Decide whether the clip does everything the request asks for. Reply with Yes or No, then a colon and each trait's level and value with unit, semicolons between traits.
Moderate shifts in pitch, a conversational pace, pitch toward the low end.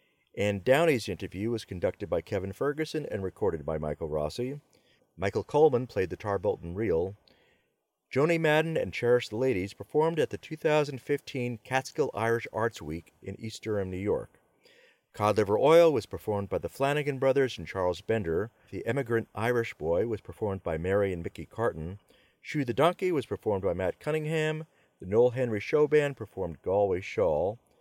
No: wide, 7.1 semitones; average, 165 wpm; low, 120 Hz